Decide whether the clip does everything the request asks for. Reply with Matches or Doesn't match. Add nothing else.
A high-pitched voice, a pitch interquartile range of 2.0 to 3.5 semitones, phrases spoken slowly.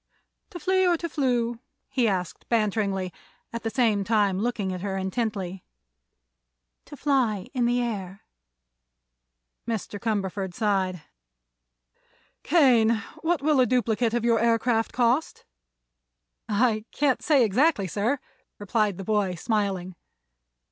Doesn't match